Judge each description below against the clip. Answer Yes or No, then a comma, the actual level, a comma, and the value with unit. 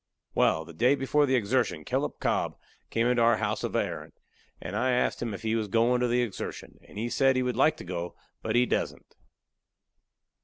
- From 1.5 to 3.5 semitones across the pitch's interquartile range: Yes, narrow, 2.6 semitones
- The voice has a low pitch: Yes, low, 120 Hz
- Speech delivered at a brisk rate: Yes, fast, 215 wpm